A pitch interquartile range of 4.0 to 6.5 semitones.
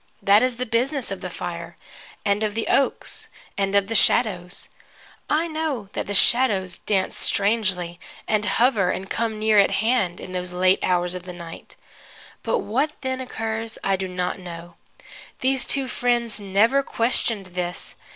Yes: average, 4.8 semitones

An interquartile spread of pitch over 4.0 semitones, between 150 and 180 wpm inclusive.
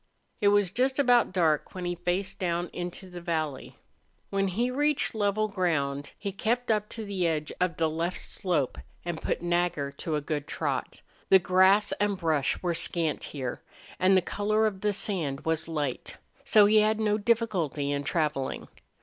Yes: average, 4.4 semitones; average, 175 wpm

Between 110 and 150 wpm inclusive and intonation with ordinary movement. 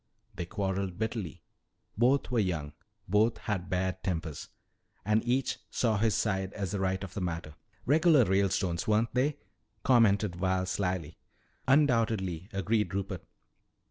Yes: average, 140 wpm; average, 3.6 semitones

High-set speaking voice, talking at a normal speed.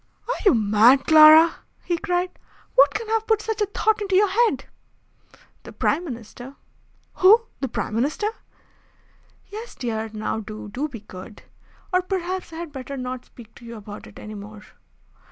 Yes: very high, 285 Hz; average, 170 wpm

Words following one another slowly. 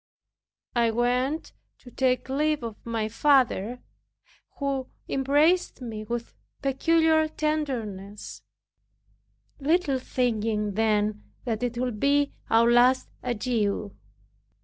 Yes: slow, 100 wpm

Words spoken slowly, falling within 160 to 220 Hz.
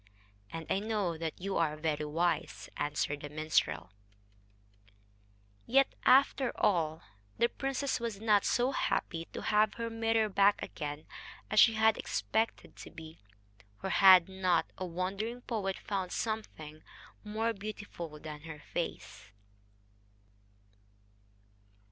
Yes: slow, 125 wpm; high, 190 Hz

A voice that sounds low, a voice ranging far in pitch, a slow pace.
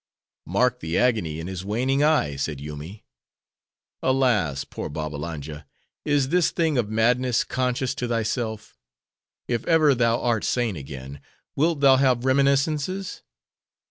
Yes: low, 120 Hz; wide, 8.6 semitones; slow, 125 wpm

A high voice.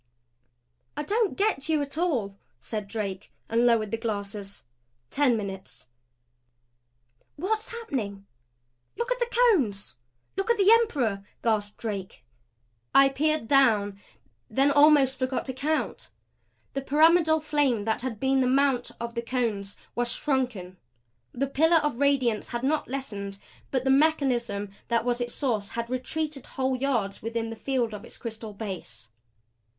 Yes: very high, 250 Hz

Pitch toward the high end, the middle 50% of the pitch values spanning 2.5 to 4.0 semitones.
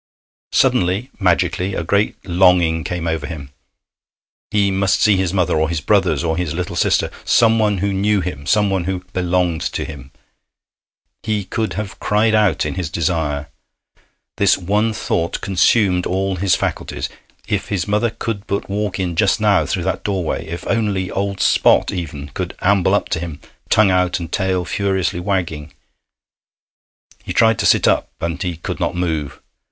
No: very low, 90 Hz; average, 3.0 semitones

